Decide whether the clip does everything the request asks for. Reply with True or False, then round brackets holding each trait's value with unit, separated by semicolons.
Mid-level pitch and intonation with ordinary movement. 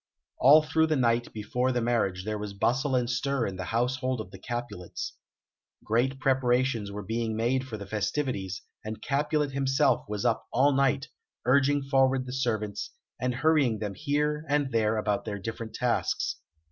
False (125 Hz; 3.9 semitones)